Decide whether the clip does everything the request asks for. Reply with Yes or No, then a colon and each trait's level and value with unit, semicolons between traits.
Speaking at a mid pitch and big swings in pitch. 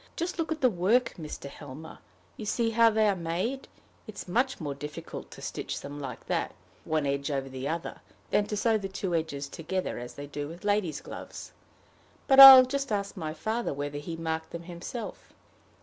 Yes: medium, 175 Hz; wide, 7.1 semitones